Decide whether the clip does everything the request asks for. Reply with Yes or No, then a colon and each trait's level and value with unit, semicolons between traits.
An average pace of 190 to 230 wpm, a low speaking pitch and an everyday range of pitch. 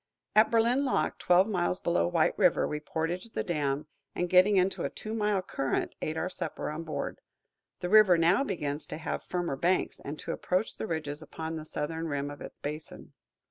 No: average, 195 wpm; medium, 170 Hz; average, 3.7 semitones